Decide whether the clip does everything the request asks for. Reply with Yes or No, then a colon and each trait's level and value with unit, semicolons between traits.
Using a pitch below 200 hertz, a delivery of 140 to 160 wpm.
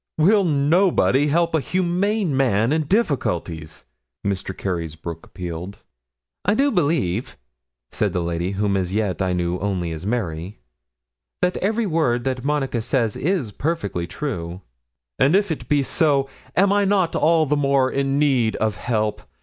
Yes: low, 135 Hz; average, 150 wpm